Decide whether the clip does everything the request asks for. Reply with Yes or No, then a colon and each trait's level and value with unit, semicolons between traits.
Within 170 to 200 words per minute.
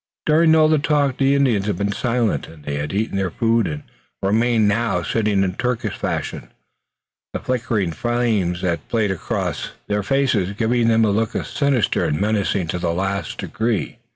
Yes: average, 175 wpm